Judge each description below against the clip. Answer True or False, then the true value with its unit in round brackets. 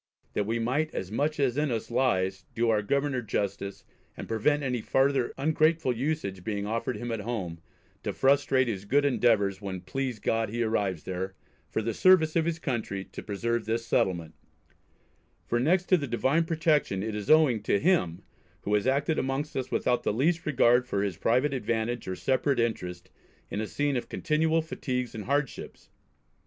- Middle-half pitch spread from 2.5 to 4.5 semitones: False (5.6 semitones)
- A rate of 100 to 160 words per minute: False (180 wpm)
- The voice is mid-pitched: False (120 Hz)